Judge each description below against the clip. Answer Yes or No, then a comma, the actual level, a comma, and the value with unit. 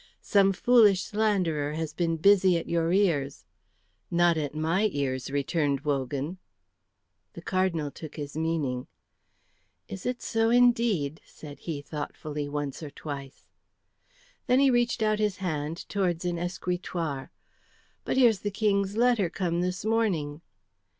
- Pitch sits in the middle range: Yes, medium, 170 Hz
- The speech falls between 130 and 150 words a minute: Yes, slow, 135 wpm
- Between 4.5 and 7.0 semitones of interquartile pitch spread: Yes, wide, 5.5 semitones